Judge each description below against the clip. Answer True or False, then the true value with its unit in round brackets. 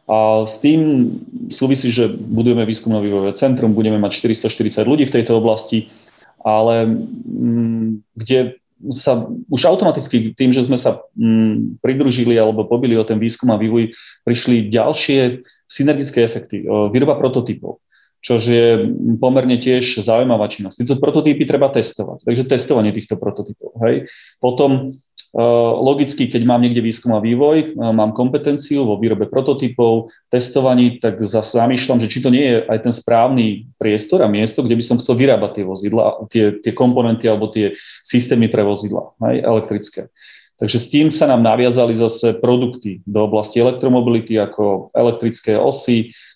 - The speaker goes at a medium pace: True (145 wpm)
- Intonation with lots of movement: False (2.5 semitones)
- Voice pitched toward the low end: True (115 Hz)